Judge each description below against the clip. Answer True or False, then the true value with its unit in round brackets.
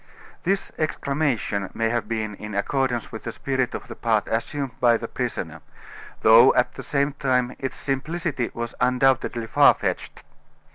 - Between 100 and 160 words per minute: True (155 wpm)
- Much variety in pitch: False (3.2 semitones)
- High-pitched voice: False (125 Hz)